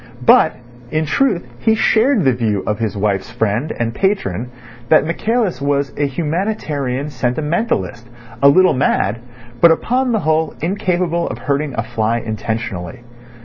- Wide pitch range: Yes, wide, 7.4 semitones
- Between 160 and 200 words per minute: No, average, 145 wpm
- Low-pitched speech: No, medium, 145 Hz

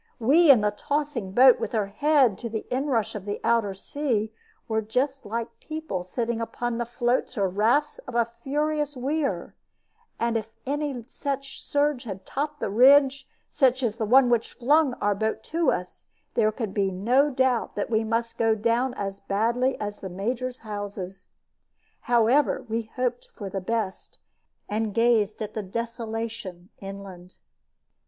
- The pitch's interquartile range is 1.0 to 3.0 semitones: No, average, 4.0 semitones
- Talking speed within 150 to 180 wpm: Yes, average, 160 wpm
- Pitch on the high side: Yes, high, 230 Hz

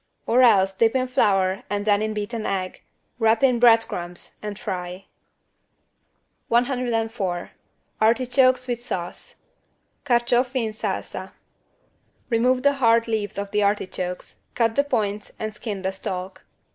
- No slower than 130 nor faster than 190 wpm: Yes, slow, 135 wpm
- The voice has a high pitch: Yes, high, 220 Hz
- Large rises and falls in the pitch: No, average, 3.6 semitones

